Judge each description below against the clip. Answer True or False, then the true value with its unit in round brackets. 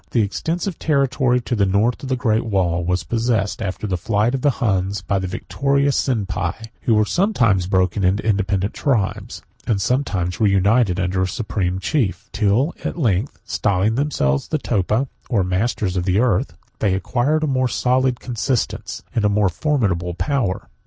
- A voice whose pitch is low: True (105 Hz)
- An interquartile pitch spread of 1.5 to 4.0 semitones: False (5.1 semitones)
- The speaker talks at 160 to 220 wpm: True (165 wpm)